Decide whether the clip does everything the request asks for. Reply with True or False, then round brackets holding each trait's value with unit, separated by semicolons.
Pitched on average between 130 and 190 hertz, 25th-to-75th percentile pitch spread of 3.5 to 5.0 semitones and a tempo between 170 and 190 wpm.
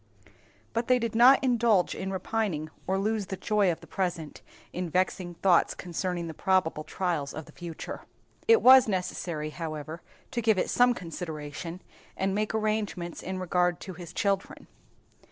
False (185 Hz; 4.0 semitones; 160 wpm)